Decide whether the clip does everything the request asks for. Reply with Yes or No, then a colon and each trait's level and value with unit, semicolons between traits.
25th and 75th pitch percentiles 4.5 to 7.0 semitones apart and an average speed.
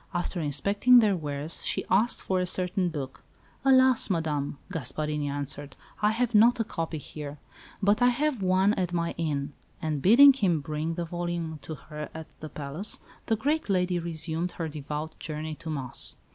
Yes: average, 4.9 semitones; average, 175 wpm